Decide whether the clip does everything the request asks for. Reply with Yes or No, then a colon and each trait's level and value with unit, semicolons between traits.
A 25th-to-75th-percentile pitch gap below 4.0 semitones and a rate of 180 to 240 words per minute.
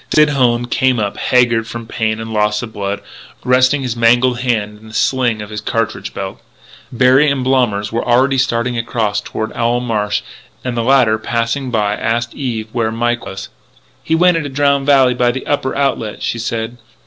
Yes: average, 2.7 semitones; average, 185 wpm